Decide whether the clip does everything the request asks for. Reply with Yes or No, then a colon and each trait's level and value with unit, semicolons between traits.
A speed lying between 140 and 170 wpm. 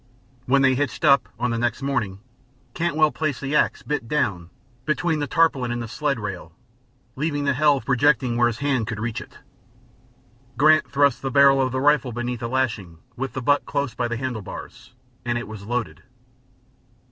No: average, 185 wpm